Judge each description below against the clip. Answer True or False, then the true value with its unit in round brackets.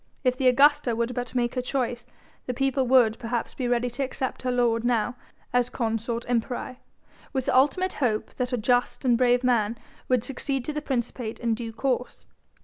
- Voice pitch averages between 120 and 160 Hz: False (245 Hz)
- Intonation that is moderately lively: False (1.6 semitones)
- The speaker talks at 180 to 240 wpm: True (190 wpm)